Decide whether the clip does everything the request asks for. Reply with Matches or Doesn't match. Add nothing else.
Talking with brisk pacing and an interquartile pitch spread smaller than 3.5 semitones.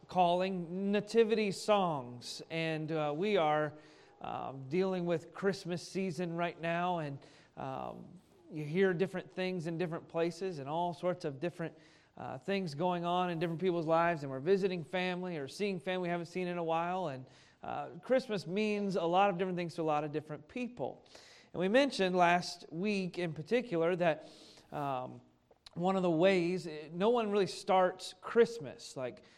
Doesn't match